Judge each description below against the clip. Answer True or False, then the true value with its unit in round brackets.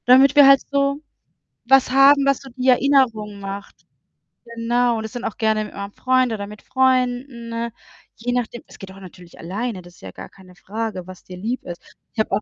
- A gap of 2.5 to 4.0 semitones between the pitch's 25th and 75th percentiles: False (4.4 semitones)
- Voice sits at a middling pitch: False (230 Hz)